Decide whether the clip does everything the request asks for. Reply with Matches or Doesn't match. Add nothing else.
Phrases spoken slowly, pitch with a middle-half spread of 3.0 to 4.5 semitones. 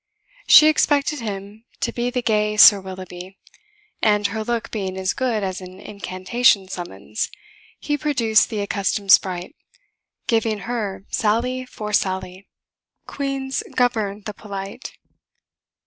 Matches